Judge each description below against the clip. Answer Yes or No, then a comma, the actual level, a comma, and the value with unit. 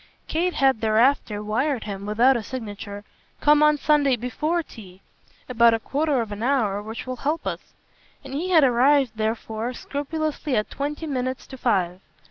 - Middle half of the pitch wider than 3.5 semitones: Yes, average, 4.9 semitones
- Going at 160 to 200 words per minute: Yes, average, 165 wpm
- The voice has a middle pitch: No, very high, 255 Hz